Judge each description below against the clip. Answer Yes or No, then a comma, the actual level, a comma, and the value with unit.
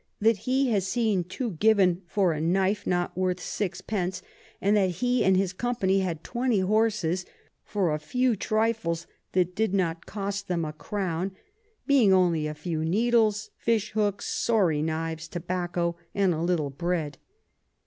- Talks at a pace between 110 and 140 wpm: No, average, 160 wpm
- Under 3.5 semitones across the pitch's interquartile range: No, average, 3.9 semitones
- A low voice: No, high, 190 Hz